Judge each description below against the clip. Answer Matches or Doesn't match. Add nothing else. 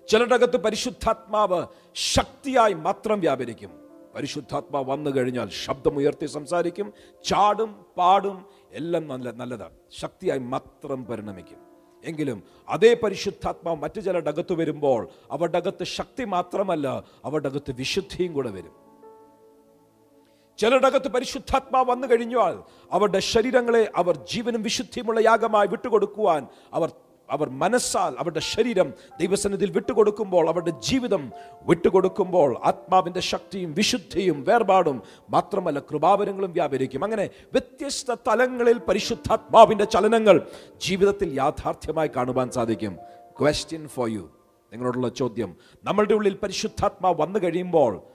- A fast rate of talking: Doesn't match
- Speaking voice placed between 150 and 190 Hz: Matches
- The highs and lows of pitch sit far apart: Matches